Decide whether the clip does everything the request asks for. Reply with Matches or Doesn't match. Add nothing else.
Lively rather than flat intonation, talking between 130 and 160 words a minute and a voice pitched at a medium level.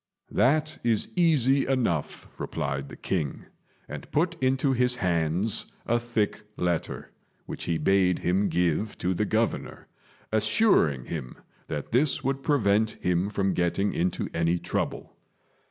Doesn't match